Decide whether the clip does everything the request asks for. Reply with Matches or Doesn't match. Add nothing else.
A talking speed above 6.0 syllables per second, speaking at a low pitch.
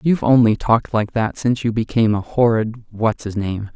Doesn't match